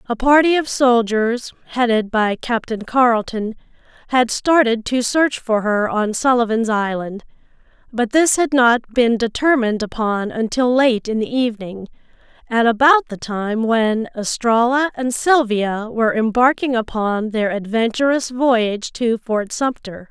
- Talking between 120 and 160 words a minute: Yes, slow, 135 wpm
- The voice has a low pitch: No, high, 235 Hz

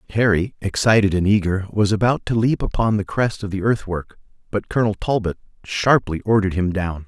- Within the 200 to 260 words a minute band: No, average, 180 wpm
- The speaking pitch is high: No, low, 100 Hz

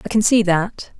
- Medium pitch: No, high, 200 Hz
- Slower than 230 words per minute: No, fast, 240 wpm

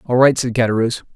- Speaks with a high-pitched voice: No, low, 120 Hz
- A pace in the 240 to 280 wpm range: No, fast, 205 wpm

